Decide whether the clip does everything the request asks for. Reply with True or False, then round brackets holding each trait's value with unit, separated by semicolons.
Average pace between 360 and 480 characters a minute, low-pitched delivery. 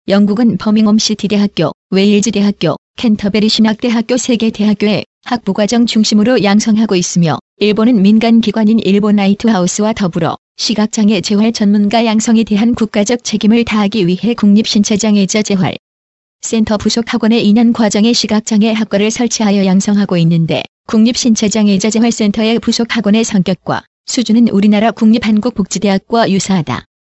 False (380 characters per minute; 215 Hz)